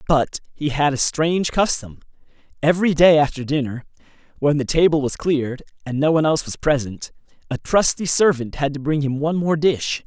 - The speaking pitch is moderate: Yes, medium, 145 Hz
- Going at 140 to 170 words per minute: No, average, 185 wpm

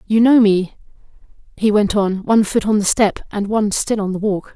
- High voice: Yes, high, 210 Hz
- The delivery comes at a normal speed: No, fast, 225 wpm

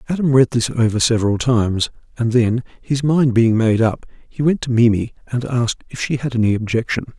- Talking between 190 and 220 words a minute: Yes, average, 200 wpm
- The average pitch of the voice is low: Yes, low, 120 Hz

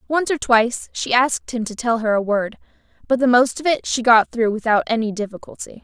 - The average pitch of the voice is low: No, high, 235 Hz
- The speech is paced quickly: Yes, fast, 225 wpm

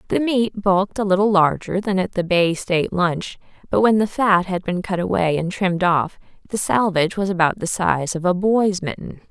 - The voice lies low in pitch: No, medium, 185 Hz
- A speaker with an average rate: No, fast, 215 wpm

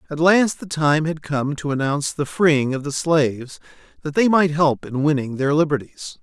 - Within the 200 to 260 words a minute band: Yes, fast, 205 wpm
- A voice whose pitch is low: No, medium, 150 Hz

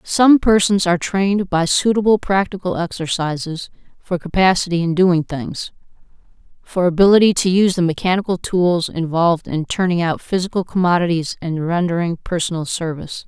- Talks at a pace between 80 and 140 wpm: Yes, slow, 135 wpm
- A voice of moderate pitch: Yes, medium, 180 Hz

